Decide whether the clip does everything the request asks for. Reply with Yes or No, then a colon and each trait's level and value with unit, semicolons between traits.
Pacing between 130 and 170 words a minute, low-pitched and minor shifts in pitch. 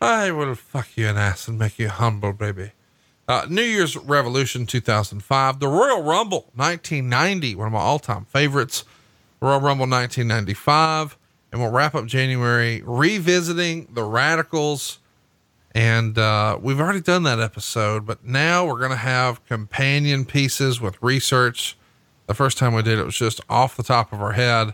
No: average, 165 wpm; low, 125 Hz; average, 4.2 semitones